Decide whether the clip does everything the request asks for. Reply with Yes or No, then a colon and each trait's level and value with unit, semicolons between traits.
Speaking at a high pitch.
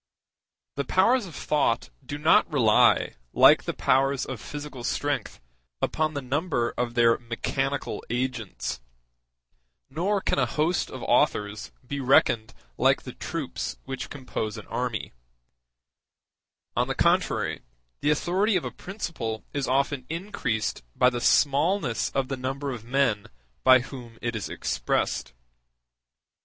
No: low, 135 Hz